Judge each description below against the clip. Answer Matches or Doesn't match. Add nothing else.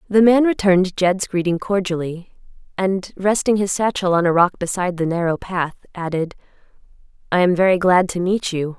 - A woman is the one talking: Matches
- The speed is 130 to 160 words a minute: Doesn't match